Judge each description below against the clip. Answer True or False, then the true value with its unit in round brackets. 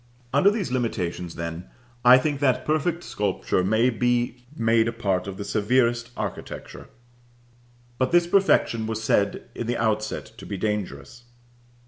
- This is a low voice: True (115 Hz)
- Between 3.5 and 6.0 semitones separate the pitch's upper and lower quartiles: True (3.8 semitones)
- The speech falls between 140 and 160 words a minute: True (145 wpm)